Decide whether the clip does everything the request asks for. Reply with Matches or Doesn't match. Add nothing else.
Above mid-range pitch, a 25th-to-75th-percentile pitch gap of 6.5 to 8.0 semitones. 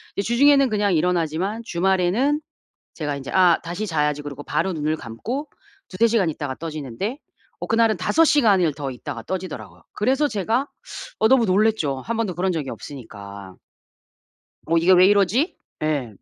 Doesn't match